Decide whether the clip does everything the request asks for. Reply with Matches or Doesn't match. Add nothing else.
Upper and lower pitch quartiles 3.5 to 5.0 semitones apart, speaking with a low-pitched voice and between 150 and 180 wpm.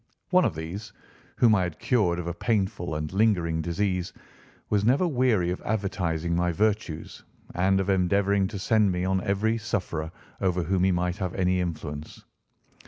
Doesn't match